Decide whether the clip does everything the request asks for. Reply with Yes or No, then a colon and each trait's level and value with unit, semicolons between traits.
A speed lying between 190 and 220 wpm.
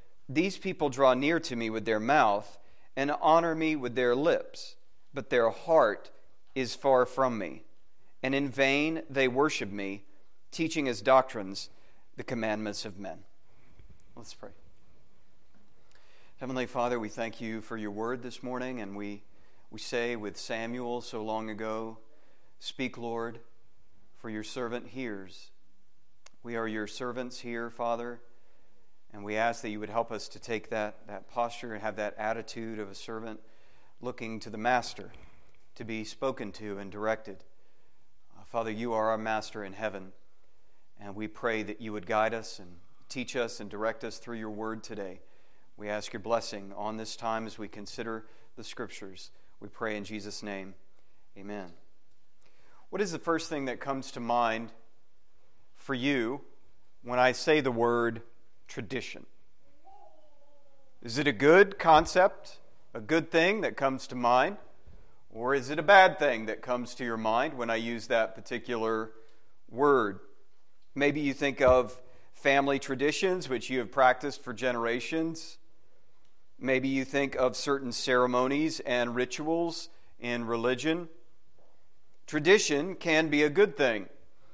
No: average, 155 wpm